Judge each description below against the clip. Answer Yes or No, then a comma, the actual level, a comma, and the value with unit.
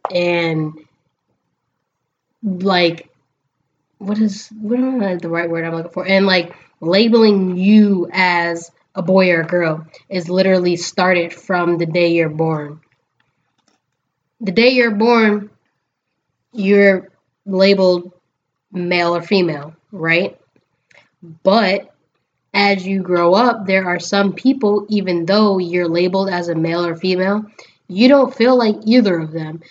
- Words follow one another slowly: Yes, slow, 130 wpm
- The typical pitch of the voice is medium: Yes, medium, 180 Hz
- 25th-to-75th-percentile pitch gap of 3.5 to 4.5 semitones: No, average, 3.1 semitones